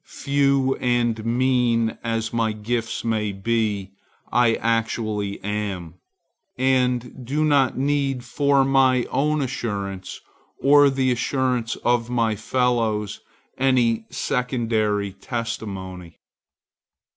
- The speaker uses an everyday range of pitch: Yes, average, 3.2 semitones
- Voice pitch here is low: Yes, low, 120 Hz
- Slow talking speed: Yes, slow, 100 wpm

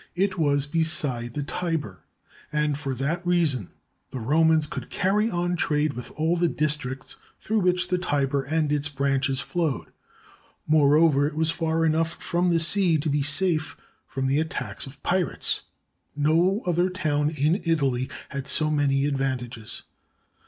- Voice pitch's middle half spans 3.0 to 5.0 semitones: Yes, average, 3.4 semitones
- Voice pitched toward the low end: No, medium, 150 Hz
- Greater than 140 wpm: Yes, average, 150 wpm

